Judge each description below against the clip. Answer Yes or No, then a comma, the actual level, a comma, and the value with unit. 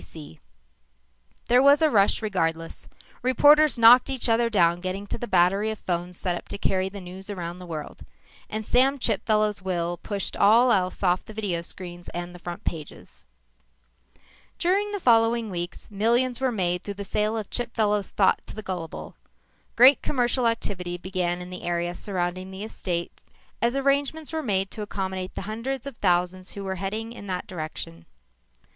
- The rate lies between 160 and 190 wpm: Yes, average, 175 wpm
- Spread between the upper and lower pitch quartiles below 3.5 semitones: No, average, 4.6 semitones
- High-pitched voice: Yes, high, 200 Hz